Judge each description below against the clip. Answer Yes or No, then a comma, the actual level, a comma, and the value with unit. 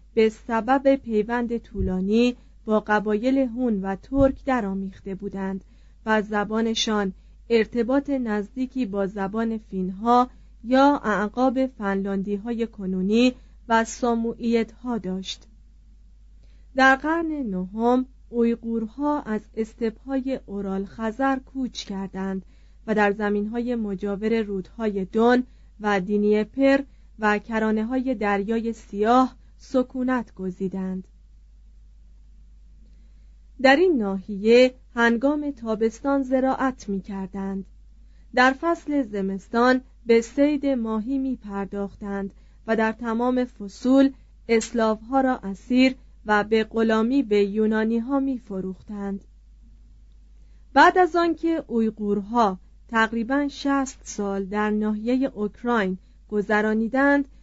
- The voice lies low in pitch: No, high, 225 Hz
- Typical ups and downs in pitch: Yes, average, 4.1 semitones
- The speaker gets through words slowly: Yes, slow, 100 wpm